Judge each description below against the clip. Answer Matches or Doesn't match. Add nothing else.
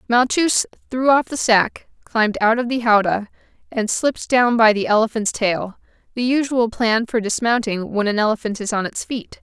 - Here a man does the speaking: Doesn't match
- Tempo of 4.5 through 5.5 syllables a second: Matches